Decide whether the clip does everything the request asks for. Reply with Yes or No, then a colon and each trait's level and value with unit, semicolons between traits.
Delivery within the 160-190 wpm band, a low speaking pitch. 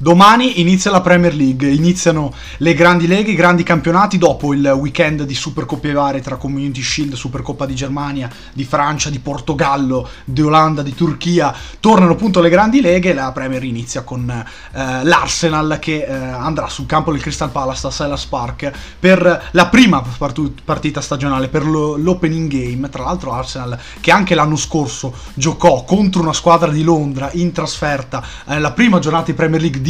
No: fast, 170 wpm; medium, 150 Hz